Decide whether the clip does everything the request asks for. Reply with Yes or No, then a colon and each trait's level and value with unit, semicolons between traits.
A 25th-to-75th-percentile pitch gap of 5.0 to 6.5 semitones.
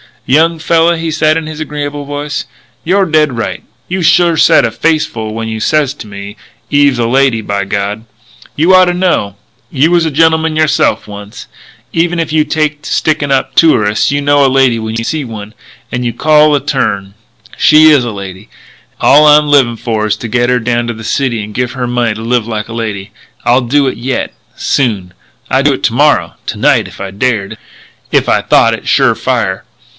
Yes: wide, 5.6 semitones